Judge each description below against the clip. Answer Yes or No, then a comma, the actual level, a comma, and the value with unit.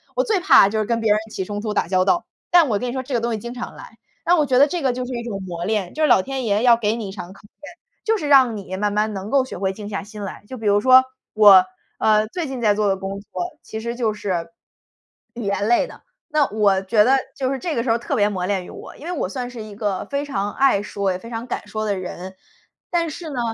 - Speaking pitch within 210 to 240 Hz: Yes, high, 220 Hz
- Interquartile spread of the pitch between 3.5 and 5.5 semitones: Yes, average, 4.4 semitones